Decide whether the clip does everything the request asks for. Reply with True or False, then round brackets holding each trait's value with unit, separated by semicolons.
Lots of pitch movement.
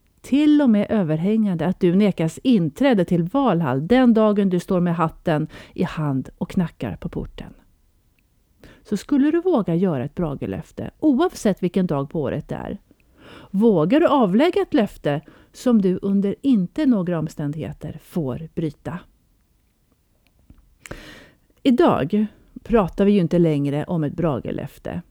True (5.8 semitones)